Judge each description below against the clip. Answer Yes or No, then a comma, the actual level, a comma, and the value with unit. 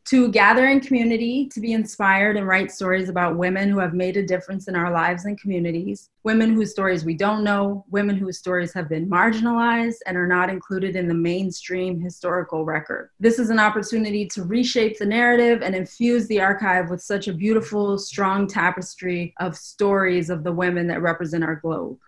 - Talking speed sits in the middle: Yes, average, 190 wpm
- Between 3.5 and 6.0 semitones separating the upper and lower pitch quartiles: No, average, 3.1 semitones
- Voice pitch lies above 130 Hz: Yes, high, 190 Hz